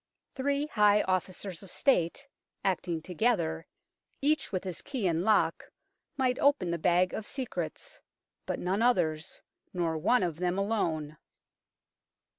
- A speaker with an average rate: No, slow, 130 wpm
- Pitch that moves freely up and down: Yes, wide, 6.3 semitones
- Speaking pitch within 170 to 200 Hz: Yes, high, 190 Hz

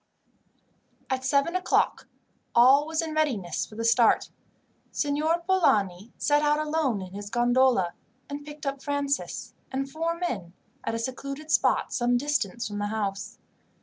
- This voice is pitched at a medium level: No, very high, 270 Hz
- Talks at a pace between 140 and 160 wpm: Yes, average, 150 wpm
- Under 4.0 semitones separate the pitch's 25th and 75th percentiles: No, average, 5.0 semitones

